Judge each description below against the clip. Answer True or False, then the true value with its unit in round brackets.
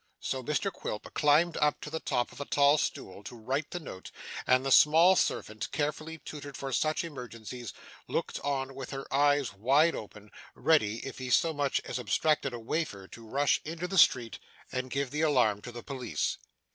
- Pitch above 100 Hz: True (135 Hz)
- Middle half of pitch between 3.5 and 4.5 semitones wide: True (3.9 semitones)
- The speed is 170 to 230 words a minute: True (190 wpm)